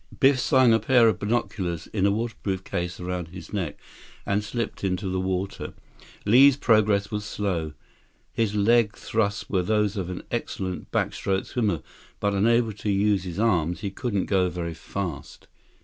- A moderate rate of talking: Yes, average, 165 wpm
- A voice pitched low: Yes, low, 100 Hz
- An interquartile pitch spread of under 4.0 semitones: Yes, average, 3.2 semitones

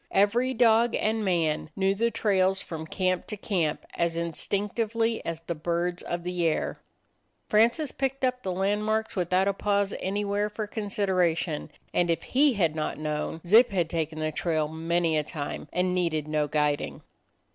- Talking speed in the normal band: Yes, average, 170 wpm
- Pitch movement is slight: No, average, 4.3 semitones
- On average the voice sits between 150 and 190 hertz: Yes, medium, 185 Hz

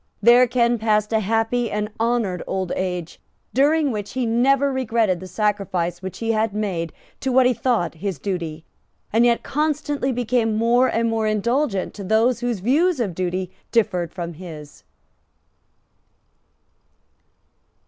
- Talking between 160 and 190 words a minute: No, average, 145 wpm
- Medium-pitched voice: No, high, 220 Hz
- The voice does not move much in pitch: No, average, 4.6 semitones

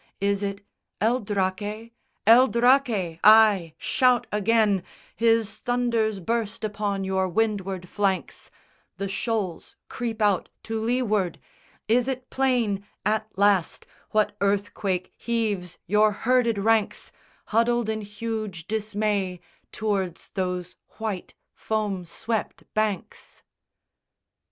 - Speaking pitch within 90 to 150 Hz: No, high, 210 Hz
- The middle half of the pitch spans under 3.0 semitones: Yes, narrow, 2.5 semitones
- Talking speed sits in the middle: No, slow, 105 wpm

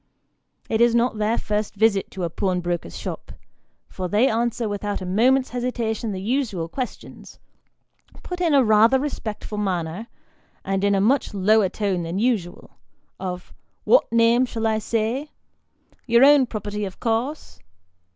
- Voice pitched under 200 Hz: No, high, 220 Hz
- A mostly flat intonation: No, average, 3.6 semitones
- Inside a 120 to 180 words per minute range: Yes, average, 150 wpm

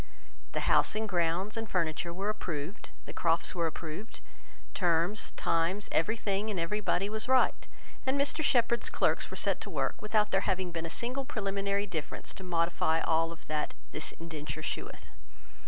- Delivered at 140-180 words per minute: Yes, average, 170 wpm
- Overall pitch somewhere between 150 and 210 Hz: Yes, medium, 185 Hz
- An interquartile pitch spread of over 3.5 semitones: Yes, average, 4.4 semitones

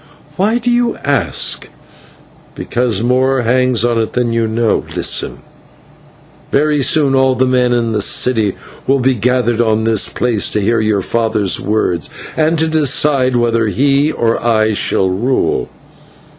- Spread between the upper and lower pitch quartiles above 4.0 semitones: No, average, 3.3 semitones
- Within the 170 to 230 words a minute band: No, average, 150 wpm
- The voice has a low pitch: Yes, low, 120 Hz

